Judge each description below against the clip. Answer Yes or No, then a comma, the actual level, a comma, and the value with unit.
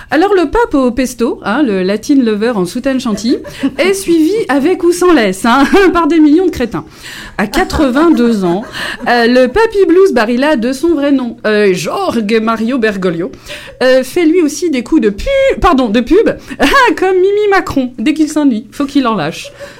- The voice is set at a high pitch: Yes, very high, 275 Hz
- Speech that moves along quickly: No, average, 190 wpm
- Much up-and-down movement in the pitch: Yes, wide, 6.6 semitones